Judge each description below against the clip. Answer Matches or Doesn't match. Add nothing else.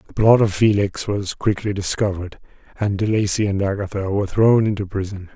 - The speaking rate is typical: Matches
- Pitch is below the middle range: Matches